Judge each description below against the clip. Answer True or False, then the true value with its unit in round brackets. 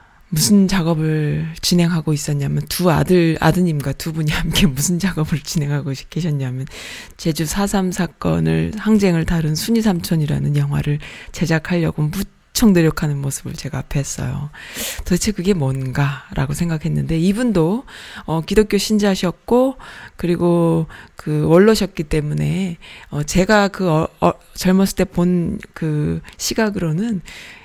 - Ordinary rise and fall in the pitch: True (4.0 semitones)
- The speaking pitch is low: False (165 Hz)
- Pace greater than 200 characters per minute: True (280 characters per minute)